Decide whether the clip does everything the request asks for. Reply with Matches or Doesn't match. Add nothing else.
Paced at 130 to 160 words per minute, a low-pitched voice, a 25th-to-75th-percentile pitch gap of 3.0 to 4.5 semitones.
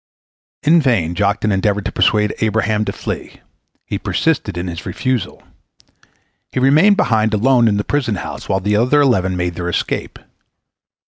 Doesn't match